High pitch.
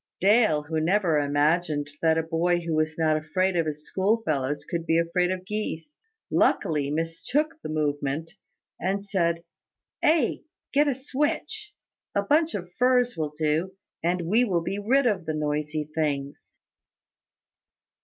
No: medium, 170 Hz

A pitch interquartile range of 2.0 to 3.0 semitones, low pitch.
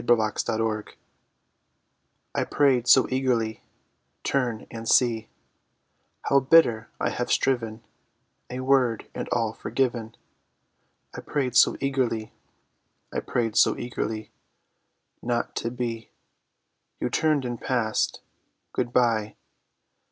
Yes: narrow, 2.4 semitones; low, 120 Hz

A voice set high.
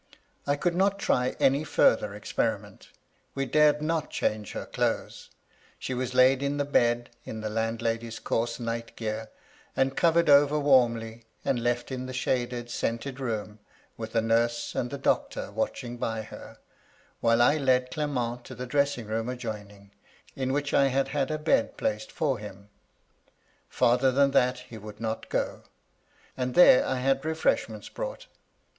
No: low, 125 Hz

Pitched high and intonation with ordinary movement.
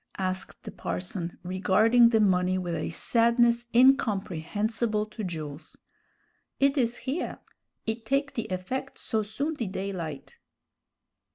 Yes: high, 215 Hz; average, 4.4 semitones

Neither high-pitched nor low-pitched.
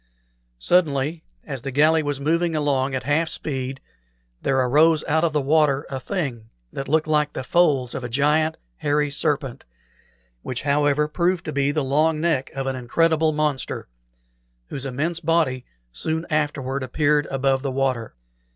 Yes: medium, 145 Hz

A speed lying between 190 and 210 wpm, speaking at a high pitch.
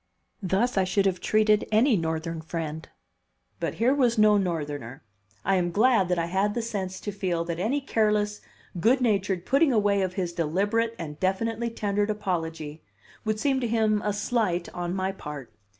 No: average, 175 wpm; high, 195 Hz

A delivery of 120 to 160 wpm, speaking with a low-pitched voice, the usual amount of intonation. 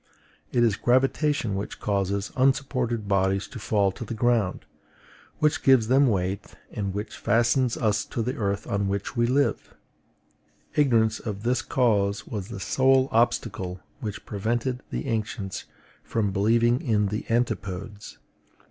Yes: average, 140 wpm; low, 110 Hz; average, 3.5 semitones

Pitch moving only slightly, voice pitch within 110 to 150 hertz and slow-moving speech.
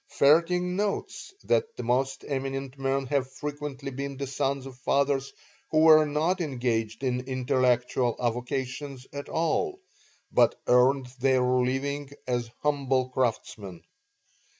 Yes: narrow, 2.2 semitones; low, 135 Hz; slow, 125 wpm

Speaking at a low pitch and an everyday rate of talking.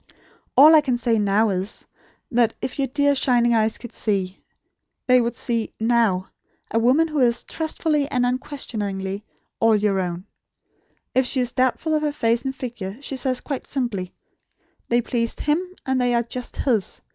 No: high, 240 Hz; average, 170 wpm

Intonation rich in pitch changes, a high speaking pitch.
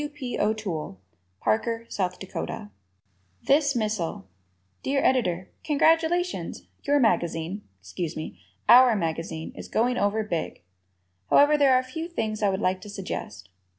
Yes: wide, 7.4 semitones; high, 215 Hz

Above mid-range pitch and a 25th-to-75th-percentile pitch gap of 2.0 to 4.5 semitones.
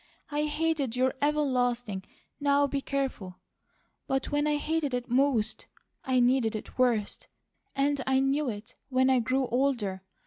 Yes: very high, 265 Hz; average, 2.7 semitones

